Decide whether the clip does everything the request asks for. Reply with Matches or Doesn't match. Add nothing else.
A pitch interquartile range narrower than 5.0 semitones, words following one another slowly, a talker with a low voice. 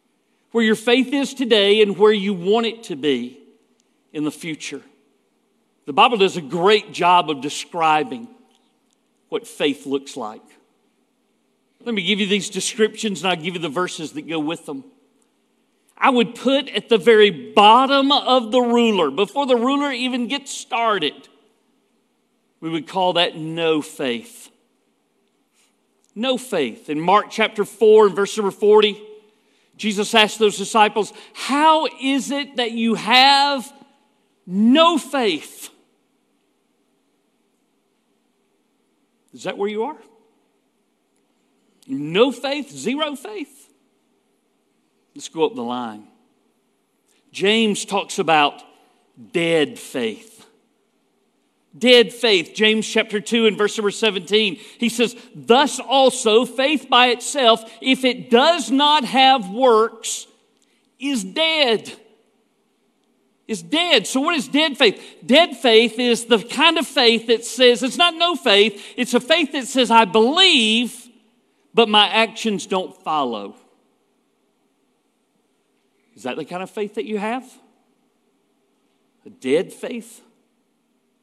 Doesn't match